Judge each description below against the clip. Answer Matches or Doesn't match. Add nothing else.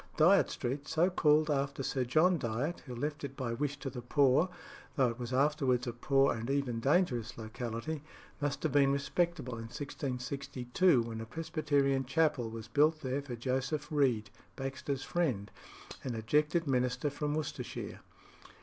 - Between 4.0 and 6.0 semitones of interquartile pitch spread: Doesn't match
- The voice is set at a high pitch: Doesn't match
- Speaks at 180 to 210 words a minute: Doesn't match